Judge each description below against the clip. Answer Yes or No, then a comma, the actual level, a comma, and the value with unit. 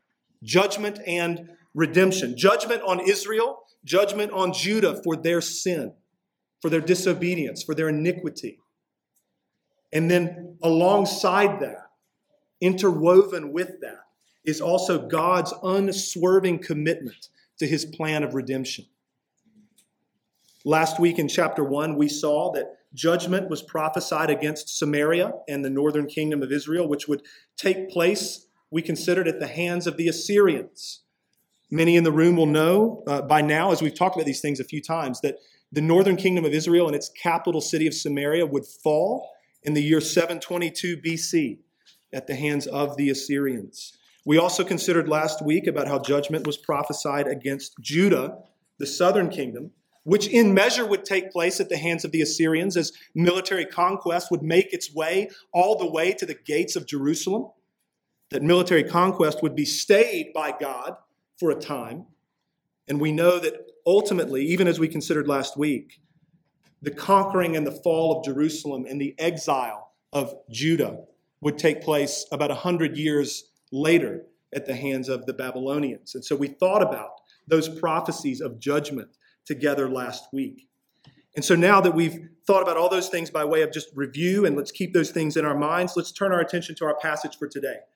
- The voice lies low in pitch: No, medium, 165 Hz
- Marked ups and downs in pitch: No, average, 3.5 semitones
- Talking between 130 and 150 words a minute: No, average, 165 wpm